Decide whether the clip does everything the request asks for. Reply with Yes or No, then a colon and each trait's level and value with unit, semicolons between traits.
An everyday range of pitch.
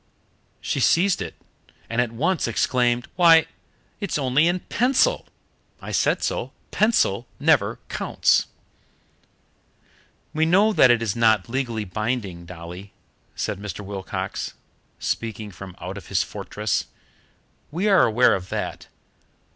No: wide, 8.3 semitones